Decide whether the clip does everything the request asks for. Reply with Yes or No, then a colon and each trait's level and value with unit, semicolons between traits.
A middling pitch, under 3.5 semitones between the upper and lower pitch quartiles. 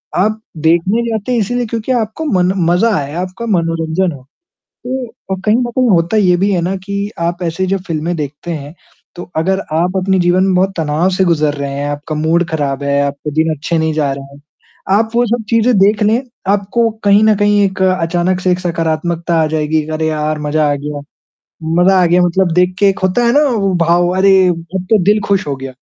No: medium, 180 Hz; average, 4.1 semitones